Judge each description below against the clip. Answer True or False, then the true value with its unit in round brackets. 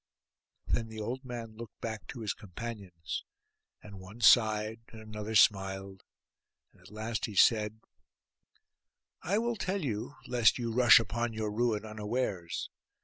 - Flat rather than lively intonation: True (2.2 semitones)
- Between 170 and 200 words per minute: False (140 wpm)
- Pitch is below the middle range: True (110 Hz)